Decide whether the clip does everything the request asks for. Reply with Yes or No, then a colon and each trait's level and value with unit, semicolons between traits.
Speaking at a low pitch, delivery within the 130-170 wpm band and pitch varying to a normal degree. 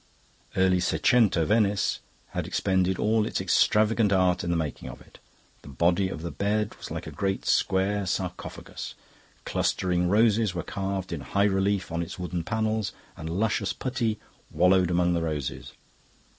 Yes: very low, 95 Hz; average, 155 wpm; average, 3.1 semitones